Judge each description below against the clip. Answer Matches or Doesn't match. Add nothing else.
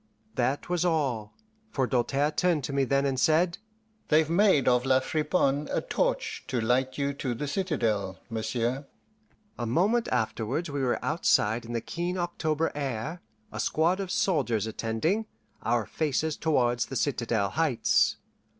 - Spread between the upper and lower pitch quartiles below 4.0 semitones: Doesn't match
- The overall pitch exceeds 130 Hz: Matches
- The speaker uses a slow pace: Doesn't match